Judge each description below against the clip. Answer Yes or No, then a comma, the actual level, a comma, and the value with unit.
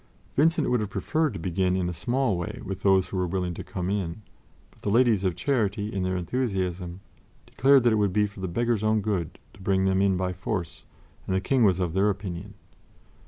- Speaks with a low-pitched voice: Yes, very low, 95 Hz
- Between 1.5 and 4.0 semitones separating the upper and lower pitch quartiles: Yes, average, 2.9 semitones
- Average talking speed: No, fast, 220 wpm